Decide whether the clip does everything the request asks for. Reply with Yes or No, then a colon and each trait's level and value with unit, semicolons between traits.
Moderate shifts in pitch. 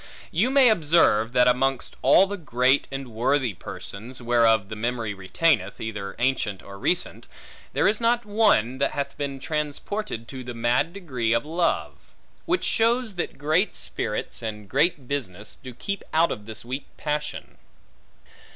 No: wide, 6.5 semitones